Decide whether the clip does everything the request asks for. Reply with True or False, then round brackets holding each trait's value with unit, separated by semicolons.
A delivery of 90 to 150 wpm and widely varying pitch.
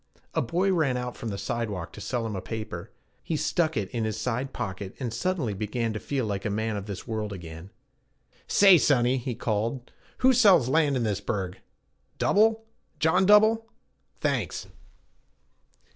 False (175 wpm; 7.0 semitones)